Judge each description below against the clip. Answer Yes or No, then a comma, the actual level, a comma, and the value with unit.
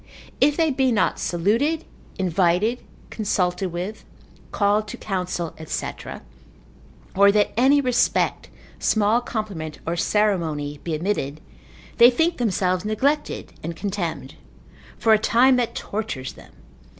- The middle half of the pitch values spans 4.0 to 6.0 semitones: Yes, average, 5.2 semitones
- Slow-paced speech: Yes, slow, 120 wpm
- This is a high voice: Yes, high, 205 Hz